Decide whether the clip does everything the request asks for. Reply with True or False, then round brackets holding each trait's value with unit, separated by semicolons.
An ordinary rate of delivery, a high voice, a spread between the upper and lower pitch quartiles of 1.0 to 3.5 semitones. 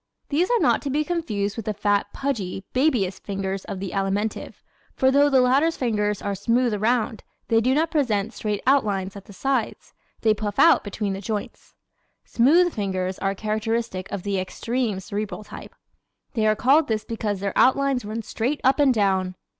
False (180 wpm; 215 Hz; 4.6 semitones)